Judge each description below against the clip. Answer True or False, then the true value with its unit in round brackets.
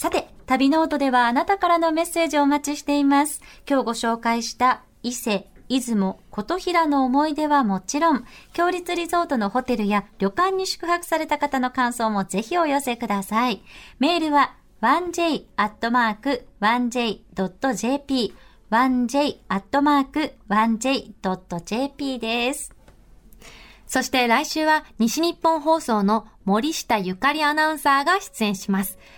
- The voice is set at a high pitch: True (265 Hz)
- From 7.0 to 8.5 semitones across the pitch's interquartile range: False (5.4 semitones)